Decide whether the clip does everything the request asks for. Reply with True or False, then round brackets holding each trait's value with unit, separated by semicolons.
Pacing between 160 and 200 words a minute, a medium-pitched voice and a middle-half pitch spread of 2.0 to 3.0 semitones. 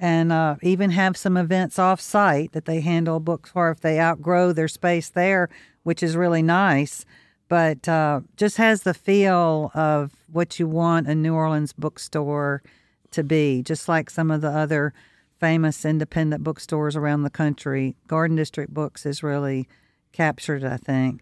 True (165 wpm; 160 Hz; 2.4 semitones)